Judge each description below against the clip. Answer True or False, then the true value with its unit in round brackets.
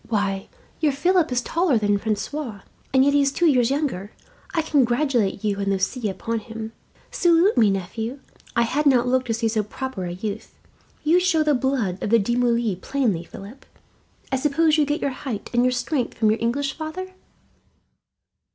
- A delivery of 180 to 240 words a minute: True (185 wpm)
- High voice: True (245 Hz)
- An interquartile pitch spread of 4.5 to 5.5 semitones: True (5.1 semitones)